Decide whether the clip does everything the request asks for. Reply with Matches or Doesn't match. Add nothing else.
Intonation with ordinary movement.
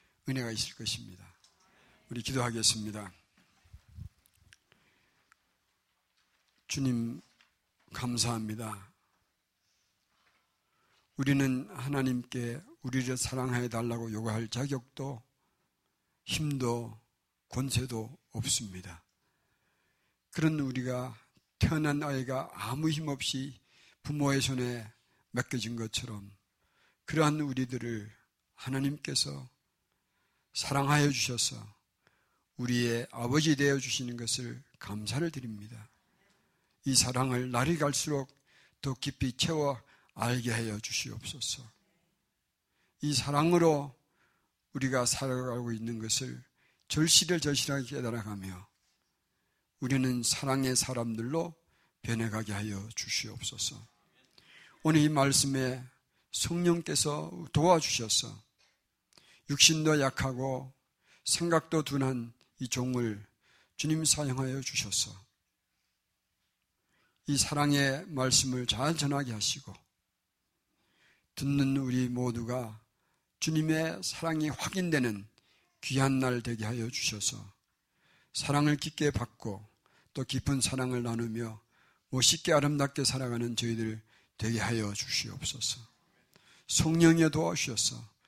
Matches